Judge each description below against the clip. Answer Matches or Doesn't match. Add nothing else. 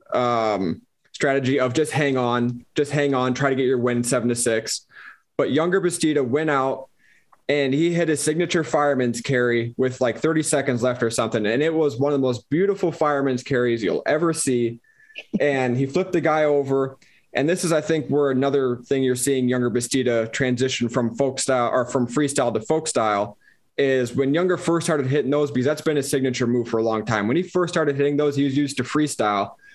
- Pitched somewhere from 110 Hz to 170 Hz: Matches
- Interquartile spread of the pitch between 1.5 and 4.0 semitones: Matches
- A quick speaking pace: Matches